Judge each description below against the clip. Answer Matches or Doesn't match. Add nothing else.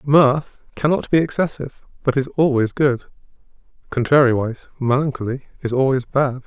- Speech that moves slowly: Matches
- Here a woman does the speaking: Doesn't match